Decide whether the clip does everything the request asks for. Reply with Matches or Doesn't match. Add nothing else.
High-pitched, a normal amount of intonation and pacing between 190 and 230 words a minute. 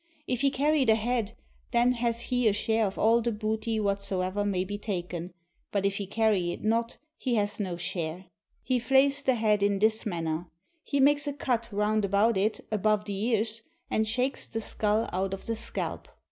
Matches